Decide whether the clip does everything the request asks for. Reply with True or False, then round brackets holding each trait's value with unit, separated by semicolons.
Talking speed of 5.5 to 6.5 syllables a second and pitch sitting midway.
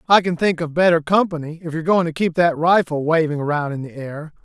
True (6.0 syllables/s; 165 Hz)